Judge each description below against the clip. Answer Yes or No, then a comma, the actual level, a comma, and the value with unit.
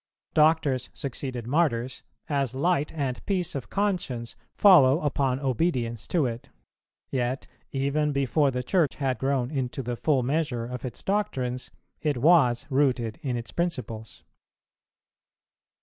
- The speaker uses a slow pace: Yes, slow, 130 wpm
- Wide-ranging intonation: No, average, 3.7 semitones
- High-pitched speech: No, low, 135 Hz